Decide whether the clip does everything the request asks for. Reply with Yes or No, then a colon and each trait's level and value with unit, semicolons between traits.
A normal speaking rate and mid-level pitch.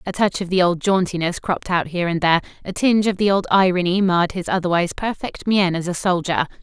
No: fast, 225 wpm; medium, 180 Hz